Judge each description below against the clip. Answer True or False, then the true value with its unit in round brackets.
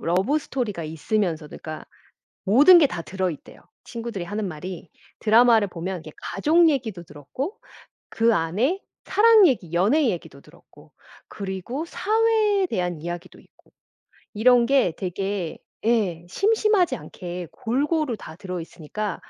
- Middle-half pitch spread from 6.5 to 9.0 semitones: True (8.0 semitones)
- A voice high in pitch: True (210 Hz)